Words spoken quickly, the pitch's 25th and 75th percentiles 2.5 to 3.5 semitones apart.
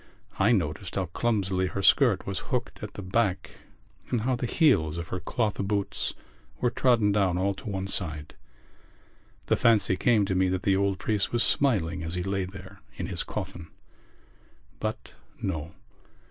No: average, 170 wpm; average, 3.0 semitones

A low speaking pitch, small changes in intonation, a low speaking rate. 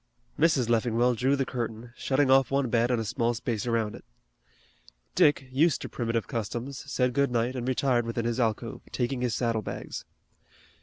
No: low, 120 Hz; narrow, 2.2 semitones; average, 175 wpm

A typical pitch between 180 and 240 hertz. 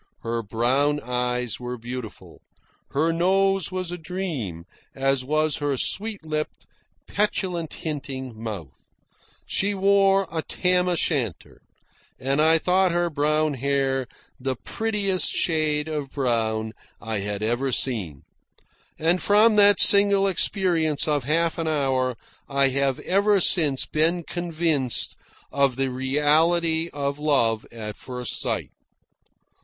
No: medium, 150 Hz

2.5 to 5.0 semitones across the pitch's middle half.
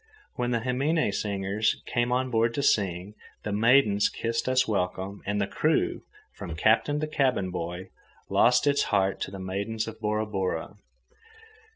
Yes: average, 4.2 semitones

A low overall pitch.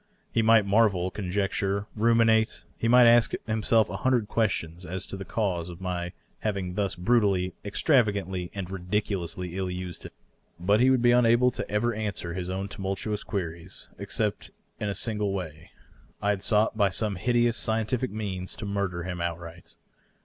Yes: low, 100 Hz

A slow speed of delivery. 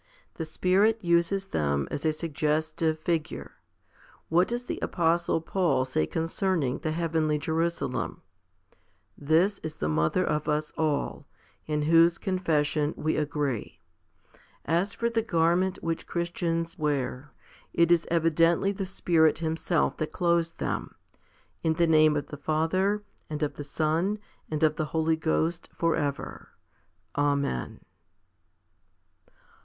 Yes: slow, 130 wpm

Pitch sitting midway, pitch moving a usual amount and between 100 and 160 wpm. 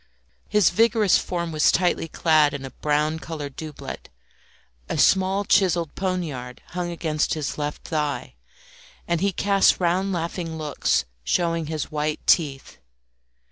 Yes: medium, 165 Hz; average, 3.3 semitones; slow, 135 wpm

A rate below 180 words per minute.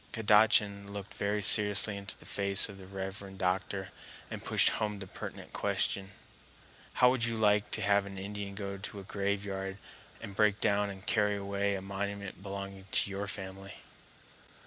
Yes: average, 170 wpm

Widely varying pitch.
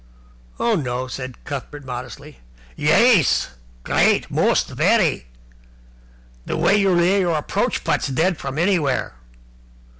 Yes: wide, 6.1 semitones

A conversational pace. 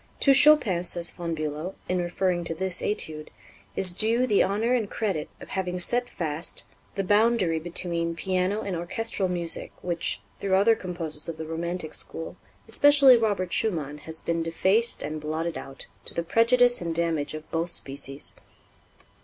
Yes: average, 160 wpm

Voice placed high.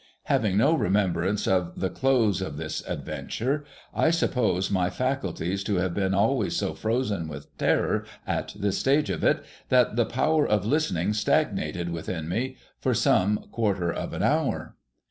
No: low, 100 Hz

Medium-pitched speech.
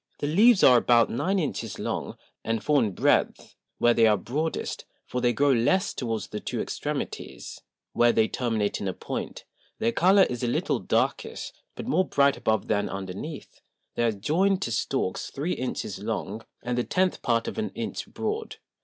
No: low, 125 Hz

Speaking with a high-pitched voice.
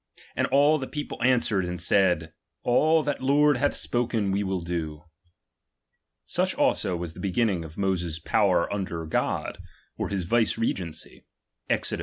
No: very low, 95 Hz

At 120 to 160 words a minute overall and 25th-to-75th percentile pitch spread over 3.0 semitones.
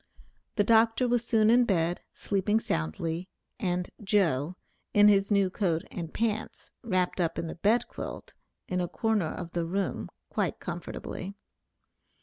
Yes: average, 145 wpm; average, 4.0 semitones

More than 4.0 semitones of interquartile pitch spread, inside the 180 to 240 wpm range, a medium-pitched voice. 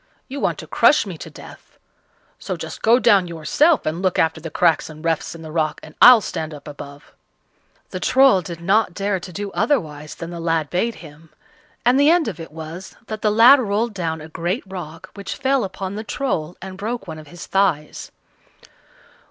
Yes: average, 5.2 semitones; average, 200 wpm; medium, 180 Hz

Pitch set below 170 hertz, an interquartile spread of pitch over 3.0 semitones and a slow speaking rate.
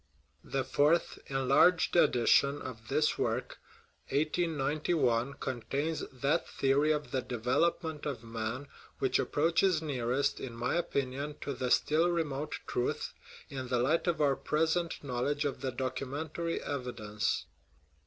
Yes: medium, 140 Hz; average, 3.5 semitones; slow, 130 wpm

